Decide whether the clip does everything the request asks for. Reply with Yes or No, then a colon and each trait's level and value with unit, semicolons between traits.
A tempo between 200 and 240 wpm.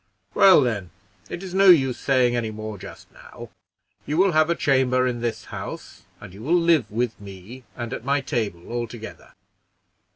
No: average, 175 wpm